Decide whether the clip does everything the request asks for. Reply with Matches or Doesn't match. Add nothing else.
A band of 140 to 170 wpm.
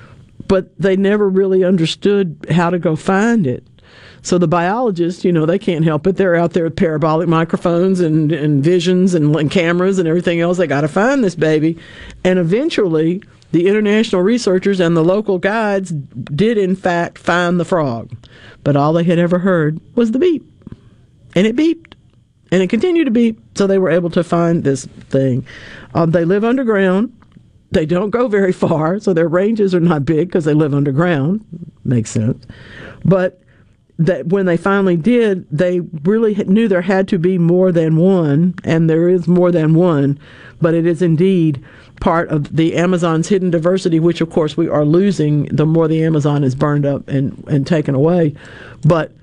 Doesn't match